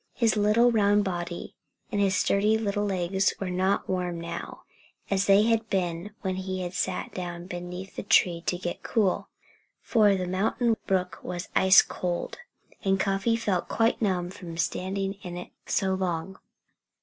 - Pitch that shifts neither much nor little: No, narrow, 2.3 semitones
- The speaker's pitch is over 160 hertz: Yes, high, 190 Hz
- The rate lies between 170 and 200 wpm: No, average, 160 wpm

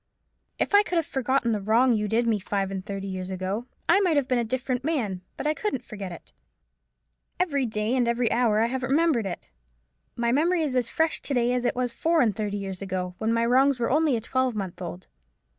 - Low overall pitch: No, high, 235 Hz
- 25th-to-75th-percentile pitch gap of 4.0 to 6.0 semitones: Yes, average, 4.4 semitones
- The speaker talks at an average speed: No, fast, 225 wpm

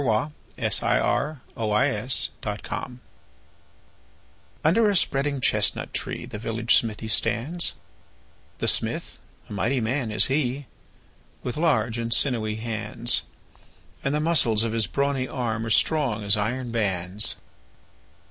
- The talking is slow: Yes, slow, 120 wpm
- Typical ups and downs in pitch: Yes, average, 4.1 semitones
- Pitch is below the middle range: Yes, low, 115 Hz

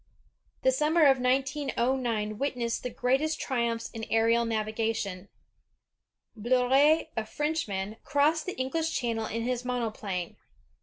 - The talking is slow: Yes, slow, 115 wpm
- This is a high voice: Yes, high, 245 Hz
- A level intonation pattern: No, average, 3.6 semitones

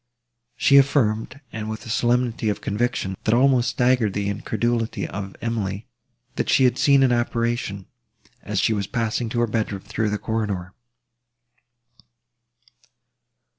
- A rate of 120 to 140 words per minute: Yes, slow, 135 wpm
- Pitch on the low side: Yes, low, 115 Hz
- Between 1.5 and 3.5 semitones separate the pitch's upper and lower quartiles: Yes, average, 2.8 semitones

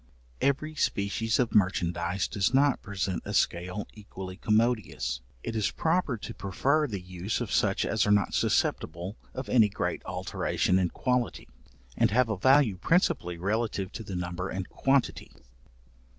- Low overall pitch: Yes, low, 105 Hz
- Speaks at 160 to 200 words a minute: No, average, 150 wpm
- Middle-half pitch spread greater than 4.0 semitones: Yes, average, 5.1 semitones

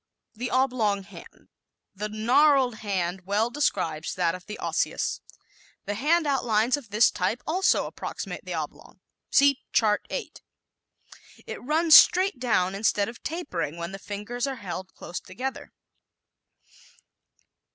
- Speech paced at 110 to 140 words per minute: Yes, slow, 135 wpm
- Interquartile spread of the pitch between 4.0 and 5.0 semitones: No, wide, 5.5 semitones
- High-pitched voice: Yes, high, 220 Hz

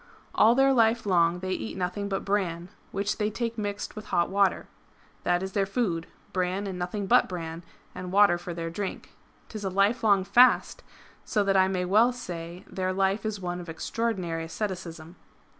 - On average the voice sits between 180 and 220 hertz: Yes, high, 190 Hz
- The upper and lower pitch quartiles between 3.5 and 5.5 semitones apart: No, average, 2.8 semitones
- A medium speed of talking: Yes, average, 180 wpm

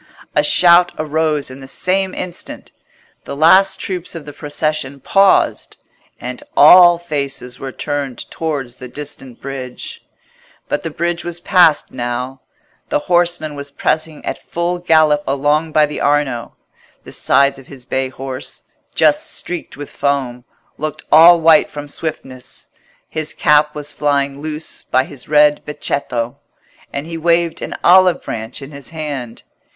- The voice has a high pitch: No, medium, 150 Hz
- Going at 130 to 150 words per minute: Yes, average, 145 wpm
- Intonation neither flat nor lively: Yes, average, 3.3 semitones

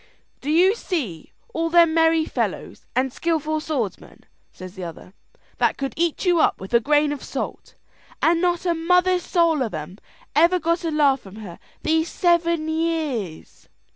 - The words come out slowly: No, average, 170 wpm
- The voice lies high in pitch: Yes, very high, 315 Hz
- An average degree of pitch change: Yes, average, 4.8 semitones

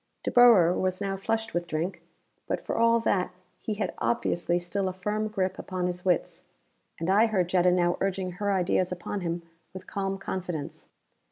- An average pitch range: No, narrow, 2.2 semitones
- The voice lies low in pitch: No, medium, 185 Hz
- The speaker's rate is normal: Yes, average, 180 wpm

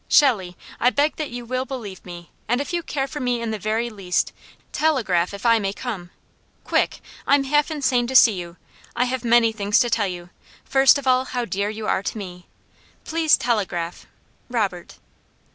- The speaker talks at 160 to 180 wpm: No, average, 190 wpm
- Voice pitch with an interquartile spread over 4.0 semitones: Yes, average, 5.0 semitones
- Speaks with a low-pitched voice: No, high, 235 Hz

